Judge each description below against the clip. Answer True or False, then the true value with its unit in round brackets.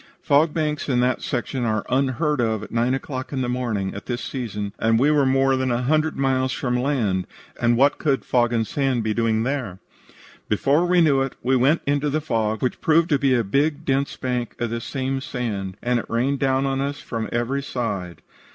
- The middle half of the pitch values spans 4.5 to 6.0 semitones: False (3.1 semitones)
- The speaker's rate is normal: False (215 wpm)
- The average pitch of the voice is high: False (130 Hz)